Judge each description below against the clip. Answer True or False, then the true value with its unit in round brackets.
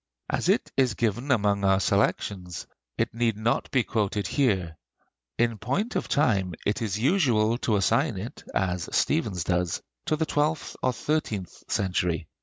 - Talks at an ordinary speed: True (155 wpm)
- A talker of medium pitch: False (105 Hz)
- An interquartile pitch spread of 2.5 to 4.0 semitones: False (4.7 semitones)